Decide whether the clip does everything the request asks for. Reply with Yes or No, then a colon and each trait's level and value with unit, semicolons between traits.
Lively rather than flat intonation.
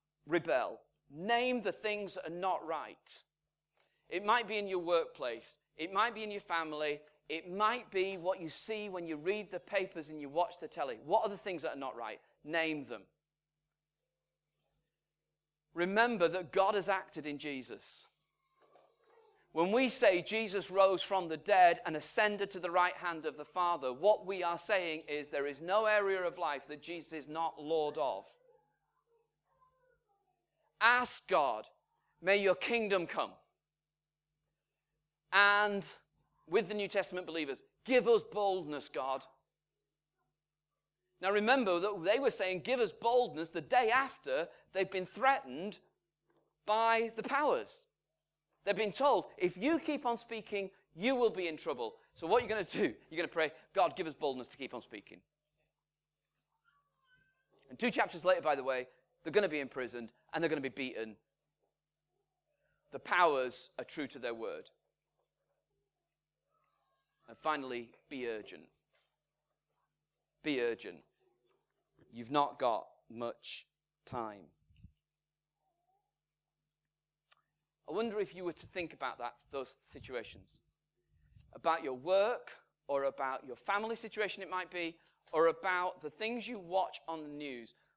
Yes: wide, 5.9 semitones